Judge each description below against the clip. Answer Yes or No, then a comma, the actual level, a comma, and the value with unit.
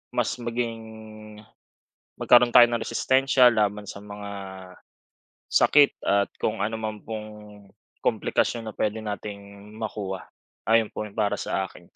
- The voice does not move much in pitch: Yes, narrow, 2.3 semitones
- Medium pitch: No, low, 110 Hz